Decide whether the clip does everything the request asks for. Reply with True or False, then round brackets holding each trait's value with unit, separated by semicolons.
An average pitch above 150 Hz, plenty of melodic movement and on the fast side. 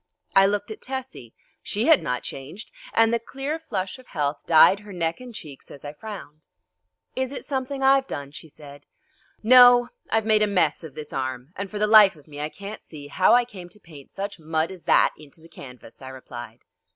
True (185 Hz; 7.3 semitones; 210 wpm)